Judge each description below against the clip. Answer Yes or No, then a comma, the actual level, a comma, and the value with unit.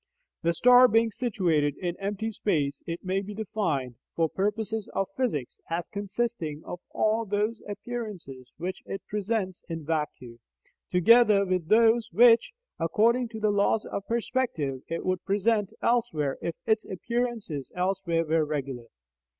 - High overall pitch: Yes, high, 195 Hz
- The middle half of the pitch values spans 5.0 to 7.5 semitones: Yes, average, 5.3 semitones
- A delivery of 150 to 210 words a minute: No, average, 140 wpm